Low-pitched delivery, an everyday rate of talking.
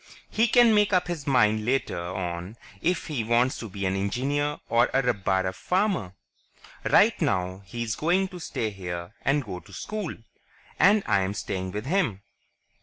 Yes: low, 115 Hz; average, 165 wpm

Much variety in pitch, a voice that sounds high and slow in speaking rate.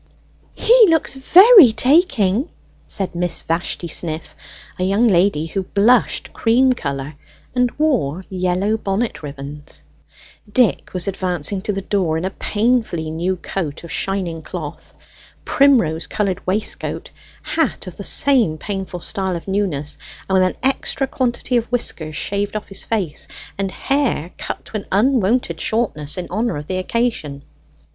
No: wide, 5.8 semitones; high, 195 Hz; average, 145 wpm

